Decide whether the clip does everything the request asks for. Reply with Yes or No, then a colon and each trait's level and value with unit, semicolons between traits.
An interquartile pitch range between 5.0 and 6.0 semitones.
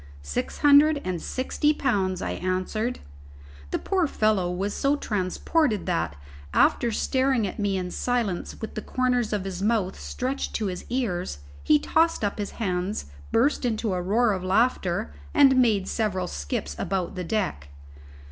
Yes: average, 5.3 semitones